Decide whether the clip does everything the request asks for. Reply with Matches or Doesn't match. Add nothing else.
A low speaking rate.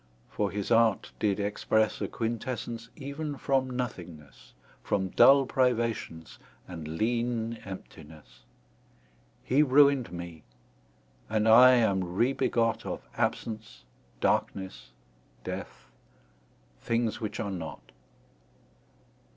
Matches